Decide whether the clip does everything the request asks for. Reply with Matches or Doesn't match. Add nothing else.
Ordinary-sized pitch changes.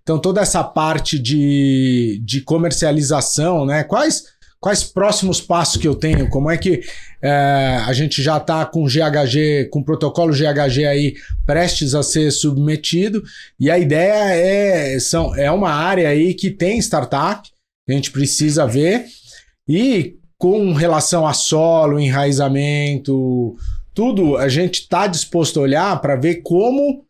Matches